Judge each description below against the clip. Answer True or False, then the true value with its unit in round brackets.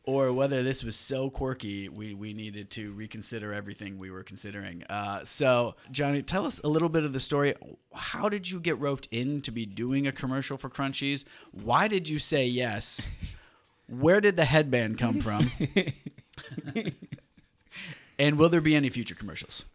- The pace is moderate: True (175 wpm)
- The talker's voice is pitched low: True (130 Hz)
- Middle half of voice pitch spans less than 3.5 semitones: False (5.5 semitones)